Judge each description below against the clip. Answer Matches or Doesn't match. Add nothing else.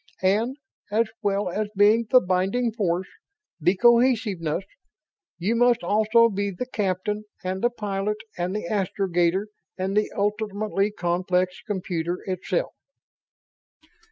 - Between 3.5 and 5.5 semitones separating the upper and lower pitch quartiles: Doesn't match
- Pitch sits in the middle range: Doesn't match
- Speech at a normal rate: Doesn't match